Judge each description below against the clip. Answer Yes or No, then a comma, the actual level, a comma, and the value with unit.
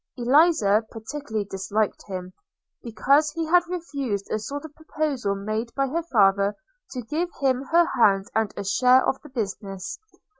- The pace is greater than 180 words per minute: No, average, 155 wpm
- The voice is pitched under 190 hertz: No, high, 240 Hz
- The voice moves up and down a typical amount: No, wide, 6.5 semitones